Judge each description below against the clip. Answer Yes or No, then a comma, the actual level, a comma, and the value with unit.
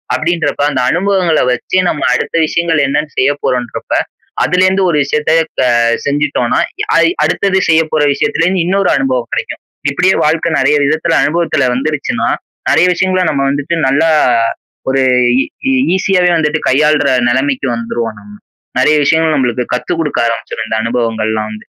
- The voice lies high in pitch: No, medium, 150 Hz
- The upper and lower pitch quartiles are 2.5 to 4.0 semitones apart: No, average, 4.7 semitones